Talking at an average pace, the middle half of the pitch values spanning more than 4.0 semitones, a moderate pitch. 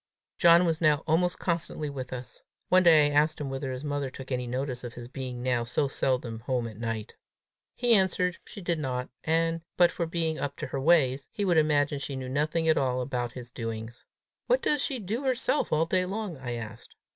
No: fast, 215 wpm; average, 4.9 semitones; medium, 145 Hz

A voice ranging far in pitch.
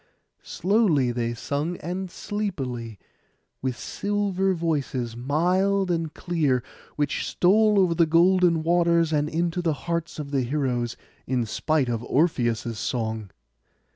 Yes: wide, 5.9 semitones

